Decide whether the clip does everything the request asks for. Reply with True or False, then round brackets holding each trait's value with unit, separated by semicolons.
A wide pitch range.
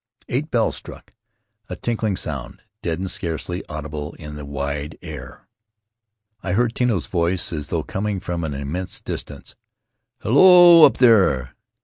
True (7.0 semitones)